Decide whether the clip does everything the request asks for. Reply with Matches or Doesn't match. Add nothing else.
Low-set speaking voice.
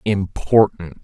Matches